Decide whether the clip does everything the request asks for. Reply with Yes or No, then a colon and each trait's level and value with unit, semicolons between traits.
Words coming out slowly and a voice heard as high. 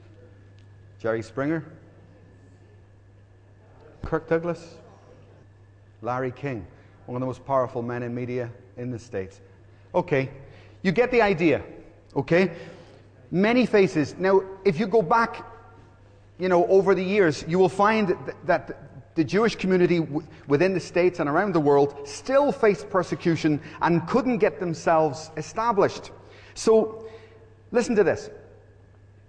No: slow, 130 wpm; medium, 140 Hz